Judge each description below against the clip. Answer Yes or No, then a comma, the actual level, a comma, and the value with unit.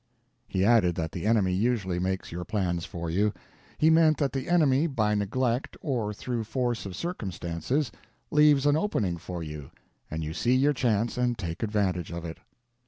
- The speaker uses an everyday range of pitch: No, wide, 6.6 semitones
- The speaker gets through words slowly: No, average, 175 wpm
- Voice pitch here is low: Yes, low, 105 Hz